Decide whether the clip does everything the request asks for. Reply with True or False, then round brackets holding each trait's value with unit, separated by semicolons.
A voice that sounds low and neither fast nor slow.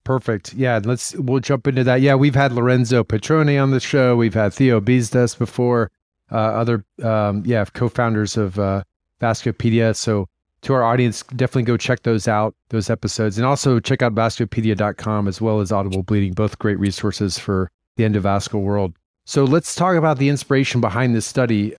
True (115 Hz; 180 wpm)